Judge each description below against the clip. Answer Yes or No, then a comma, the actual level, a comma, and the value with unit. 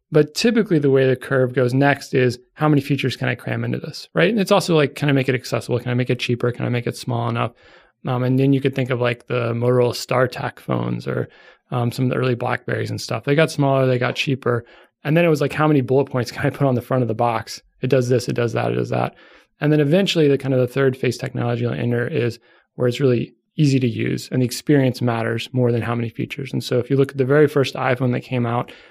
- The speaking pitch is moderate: No, low, 130 Hz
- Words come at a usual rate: No, fast, 275 wpm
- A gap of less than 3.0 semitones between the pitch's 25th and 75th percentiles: Yes, narrow, 2.6 semitones